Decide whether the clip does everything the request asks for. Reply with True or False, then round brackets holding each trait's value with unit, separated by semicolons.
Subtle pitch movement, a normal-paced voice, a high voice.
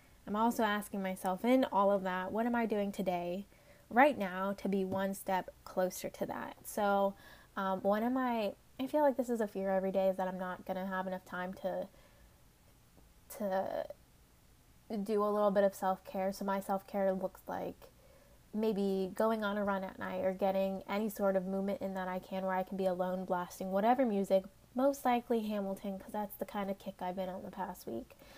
False (1.9 semitones; 210 wpm; 195 Hz)